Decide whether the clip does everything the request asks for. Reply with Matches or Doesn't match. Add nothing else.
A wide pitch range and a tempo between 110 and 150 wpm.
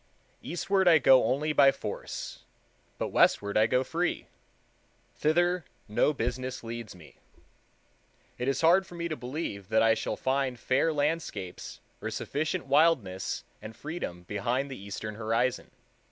Matches